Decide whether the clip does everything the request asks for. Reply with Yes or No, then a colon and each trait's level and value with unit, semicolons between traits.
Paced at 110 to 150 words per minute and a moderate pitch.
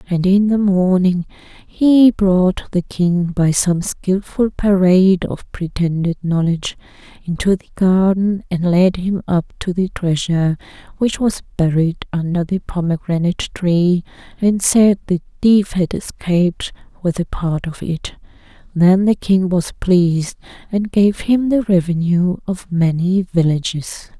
Yes: average, 140 wpm; medium, 180 Hz